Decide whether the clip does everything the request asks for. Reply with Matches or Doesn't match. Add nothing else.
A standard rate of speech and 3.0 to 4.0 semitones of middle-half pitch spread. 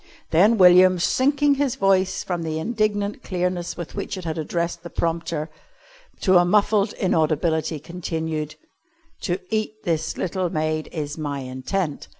Matches